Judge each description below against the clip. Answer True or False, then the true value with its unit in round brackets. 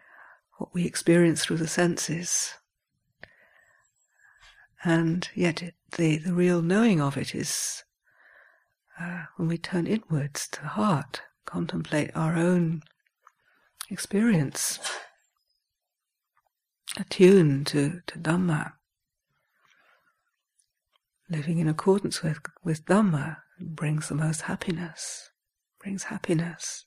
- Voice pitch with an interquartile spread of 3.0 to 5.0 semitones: False (2.5 semitones)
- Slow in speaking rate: True (100 wpm)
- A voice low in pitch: False (170 Hz)